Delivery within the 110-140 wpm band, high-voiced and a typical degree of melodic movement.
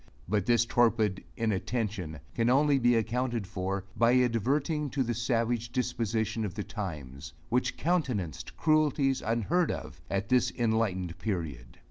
No: slow, 135 wpm; low, 115 Hz; average, 4.3 semitones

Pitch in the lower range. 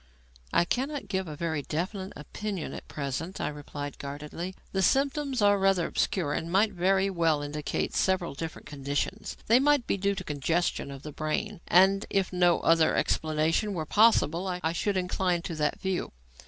No: medium, 175 Hz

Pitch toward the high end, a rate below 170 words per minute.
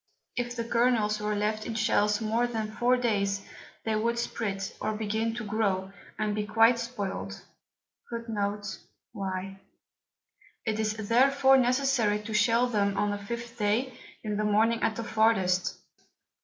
Yes: high, 220 Hz; average, 140 wpm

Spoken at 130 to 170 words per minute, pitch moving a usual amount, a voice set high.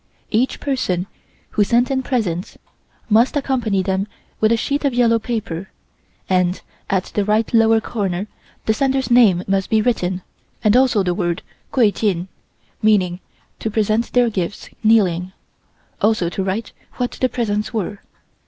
Yes: average, 150 wpm; average, 3.9 semitones; high, 215 Hz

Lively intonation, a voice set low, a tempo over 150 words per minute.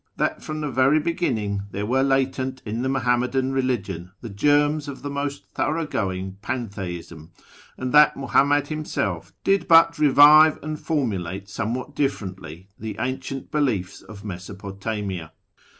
No: wide, 6.6 semitones; low, 130 Hz; average, 145 wpm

